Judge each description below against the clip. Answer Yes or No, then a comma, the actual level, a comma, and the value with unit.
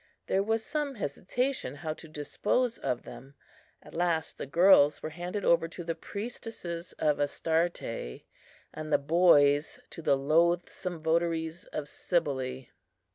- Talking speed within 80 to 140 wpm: Yes, slow, 135 wpm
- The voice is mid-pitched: Yes, medium, 165 Hz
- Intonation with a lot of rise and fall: No, average, 3.5 semitones